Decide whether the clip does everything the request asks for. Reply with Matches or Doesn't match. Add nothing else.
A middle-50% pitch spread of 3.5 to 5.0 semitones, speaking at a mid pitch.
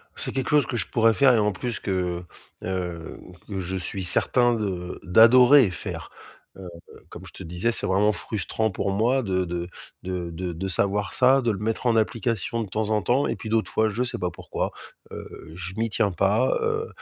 Doesn't match